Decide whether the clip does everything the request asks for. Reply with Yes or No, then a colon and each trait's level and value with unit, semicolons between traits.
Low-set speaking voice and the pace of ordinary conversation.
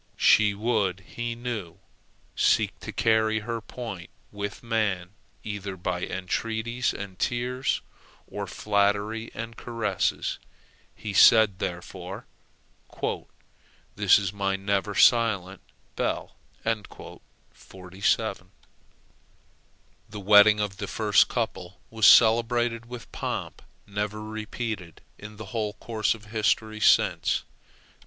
No: low, 105 Hz; slow, 105 wpm